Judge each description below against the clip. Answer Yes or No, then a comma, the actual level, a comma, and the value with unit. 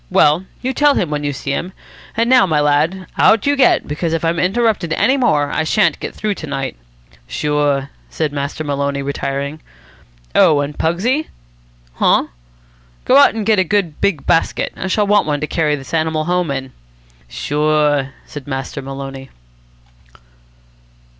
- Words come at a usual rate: Yes, average, 165 wpm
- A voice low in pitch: No, medium, 155 Hz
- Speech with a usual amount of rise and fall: Yes, average, 5.0 semitones